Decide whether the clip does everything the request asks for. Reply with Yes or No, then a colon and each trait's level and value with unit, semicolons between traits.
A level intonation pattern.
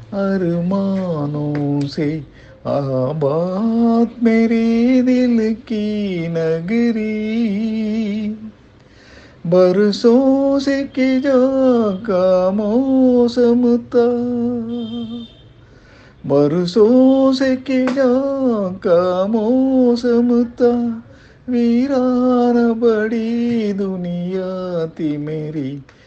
No: average, 5.0 semitones